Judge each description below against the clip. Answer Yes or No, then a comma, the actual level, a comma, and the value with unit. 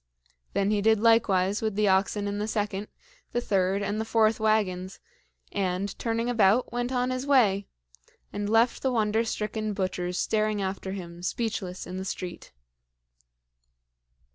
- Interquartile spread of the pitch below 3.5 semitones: Yes, narrow, 2.6 semitones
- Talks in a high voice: Yes, high, 210 Hz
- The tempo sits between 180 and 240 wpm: No, average, 150 wpm